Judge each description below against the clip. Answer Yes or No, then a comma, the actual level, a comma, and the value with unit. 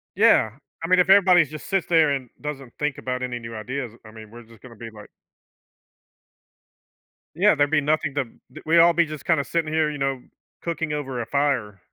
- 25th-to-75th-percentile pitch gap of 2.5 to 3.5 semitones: No, average, 4.4 semitones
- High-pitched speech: No, medium, 145 Hz